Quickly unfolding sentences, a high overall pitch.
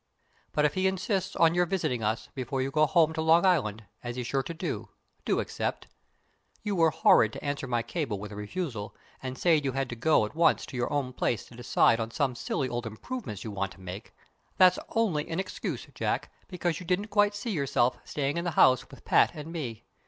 No: fast, 220 wpm; medium, 140 Hz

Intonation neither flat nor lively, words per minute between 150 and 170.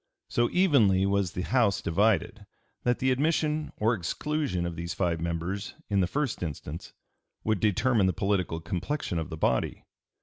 No: wide, 6.3 semitones; average, 160 wpm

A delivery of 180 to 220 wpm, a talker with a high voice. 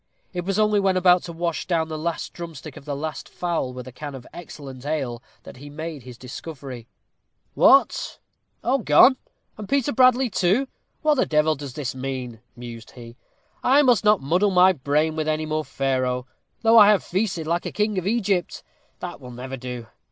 No: average, 190 wpm; medium, 155 Hz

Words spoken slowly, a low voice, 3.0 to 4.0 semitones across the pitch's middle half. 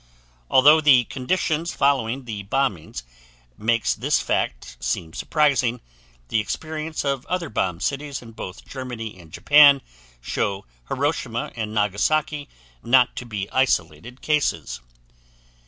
No: slow, 120 wpm; low, 125 Hz; wide, 5.5 semitones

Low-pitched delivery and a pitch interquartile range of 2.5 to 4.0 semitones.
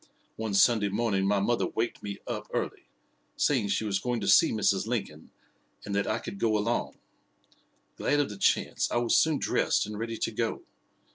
Yes: low, 110 Hz; average, 2.8 semitones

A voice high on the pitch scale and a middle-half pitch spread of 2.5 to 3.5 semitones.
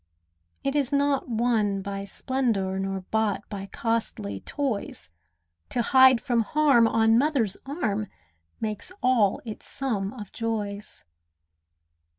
No: high, 225 Hz; average, 4.4 semitones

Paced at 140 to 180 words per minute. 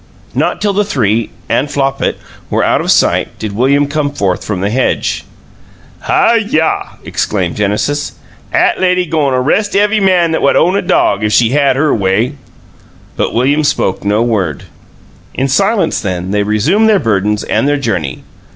Yes: average, 170 wpm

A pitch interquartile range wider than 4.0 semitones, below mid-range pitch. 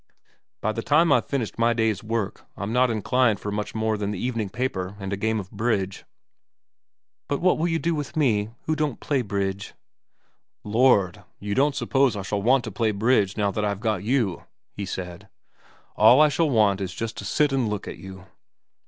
Yes: average, 4.5 semitones; low, 110 Hz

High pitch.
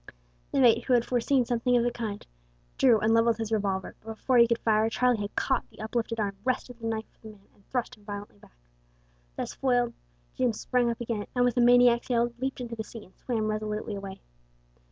Yes: high, 230 Hz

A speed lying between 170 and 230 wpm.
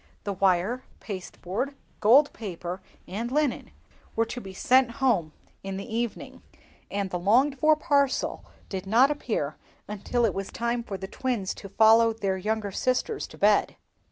No: average, 155 wpm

